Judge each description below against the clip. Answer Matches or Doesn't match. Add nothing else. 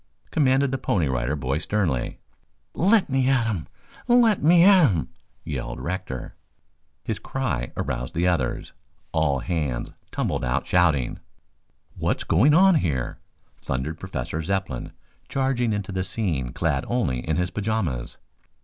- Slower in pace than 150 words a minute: Matches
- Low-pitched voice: Matches